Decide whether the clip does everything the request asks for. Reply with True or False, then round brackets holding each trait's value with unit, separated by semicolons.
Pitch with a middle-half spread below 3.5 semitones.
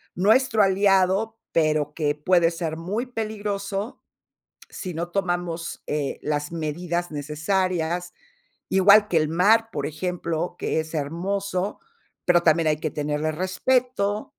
False (4.1 semitones)